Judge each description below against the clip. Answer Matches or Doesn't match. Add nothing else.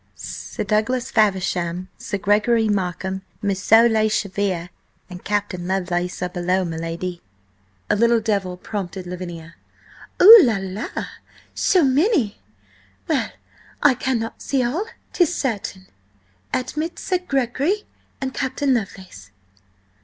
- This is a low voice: Doesn't match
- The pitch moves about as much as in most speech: Doesn't match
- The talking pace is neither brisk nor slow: Doesn't match